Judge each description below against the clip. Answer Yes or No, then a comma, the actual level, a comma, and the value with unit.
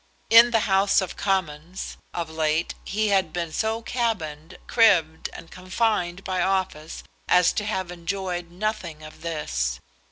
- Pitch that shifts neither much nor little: Yes, average, 3.9 semitones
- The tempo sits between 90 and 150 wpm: Yes, average, 140 wpm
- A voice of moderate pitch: Yes, medium, 180 Hz